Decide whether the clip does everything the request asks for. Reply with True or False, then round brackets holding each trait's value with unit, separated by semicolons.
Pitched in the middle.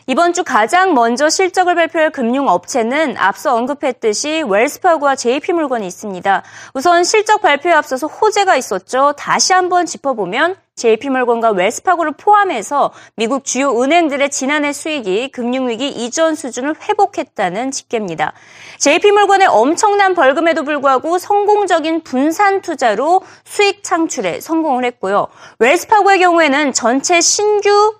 False (315 Hz)